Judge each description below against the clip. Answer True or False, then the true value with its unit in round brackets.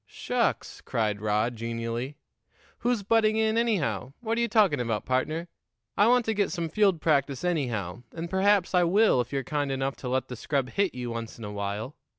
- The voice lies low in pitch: False (145 Hz)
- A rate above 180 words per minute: True (195 wpm)